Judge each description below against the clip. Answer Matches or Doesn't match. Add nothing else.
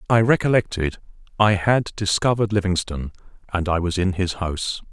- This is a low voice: Matches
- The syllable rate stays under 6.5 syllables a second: Matches